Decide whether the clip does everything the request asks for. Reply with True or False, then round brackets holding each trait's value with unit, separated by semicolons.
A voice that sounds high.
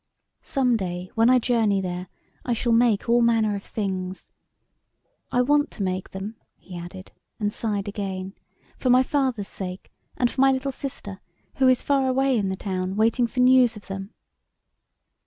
True (220 Hz)